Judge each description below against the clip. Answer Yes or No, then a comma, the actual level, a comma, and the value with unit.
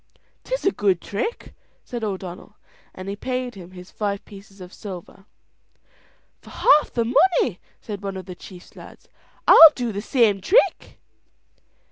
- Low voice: No, high, 205 Hz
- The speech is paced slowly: No, average, 150 wpm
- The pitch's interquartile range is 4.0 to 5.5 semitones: Yes, average, 4.6 semitones